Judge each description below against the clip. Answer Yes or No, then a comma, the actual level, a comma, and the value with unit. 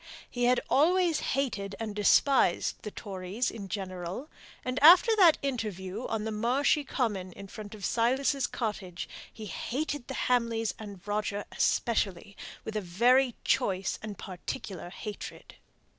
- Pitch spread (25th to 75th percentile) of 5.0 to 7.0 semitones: No, average, 4.3 semitones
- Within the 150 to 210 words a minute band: No, average, 140 wpm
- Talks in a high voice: Yes, high, 220 Hz